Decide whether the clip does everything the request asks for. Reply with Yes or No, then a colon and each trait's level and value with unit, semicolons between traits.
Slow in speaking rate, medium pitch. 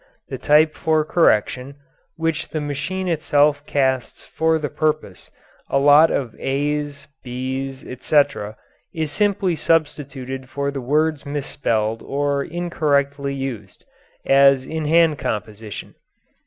Yes: slow, 115 wpm; medium, 145 Hz